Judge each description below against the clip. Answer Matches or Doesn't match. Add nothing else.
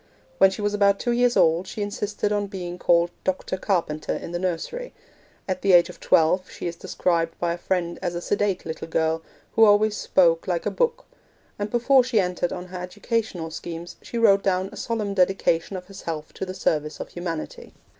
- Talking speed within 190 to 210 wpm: Matches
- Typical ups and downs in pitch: Matches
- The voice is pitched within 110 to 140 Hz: Doesn't match